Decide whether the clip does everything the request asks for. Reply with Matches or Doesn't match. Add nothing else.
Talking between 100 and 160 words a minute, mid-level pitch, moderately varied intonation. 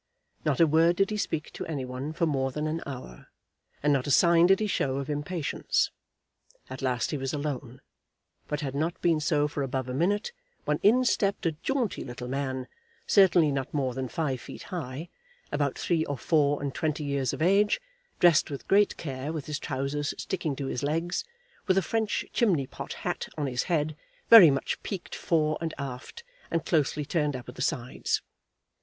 Doesn't match